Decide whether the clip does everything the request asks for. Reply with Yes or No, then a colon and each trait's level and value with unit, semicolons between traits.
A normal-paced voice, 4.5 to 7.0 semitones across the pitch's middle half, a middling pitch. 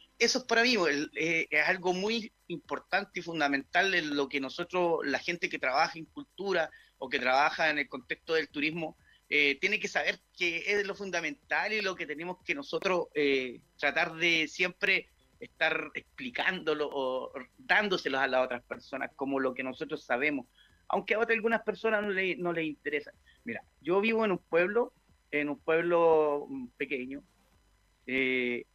Yes: average, 170 wpm; average, 4.8 semitones; medium, 160 Hz